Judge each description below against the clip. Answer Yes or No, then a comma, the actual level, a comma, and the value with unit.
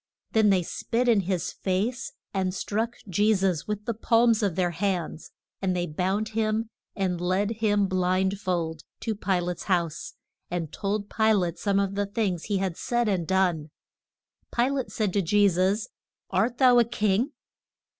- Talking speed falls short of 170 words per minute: No, average, 175 wpm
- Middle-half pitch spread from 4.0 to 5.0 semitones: No, average, 3.2 semitones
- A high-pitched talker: Yes, high, 195 Hz